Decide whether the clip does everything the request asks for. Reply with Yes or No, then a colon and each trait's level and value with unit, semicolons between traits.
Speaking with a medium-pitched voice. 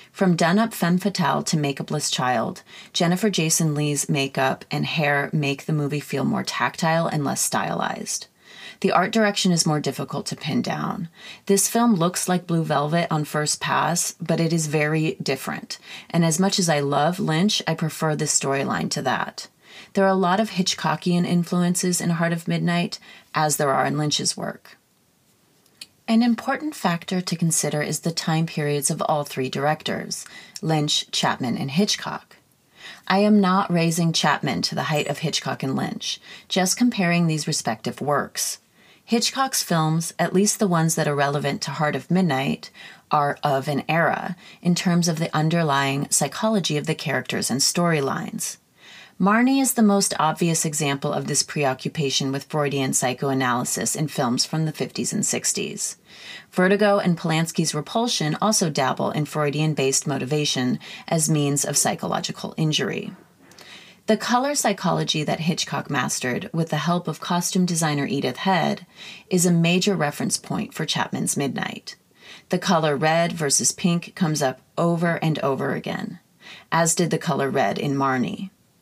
Yes: medium, 170 Hz